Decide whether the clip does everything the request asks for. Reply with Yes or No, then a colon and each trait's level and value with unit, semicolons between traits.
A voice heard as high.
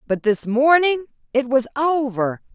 Yes: very high, 265 Hz